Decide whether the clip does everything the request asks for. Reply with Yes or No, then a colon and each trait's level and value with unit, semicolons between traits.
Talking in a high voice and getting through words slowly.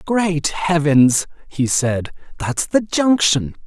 No: medium, 160 Hz; slow, 115 wpm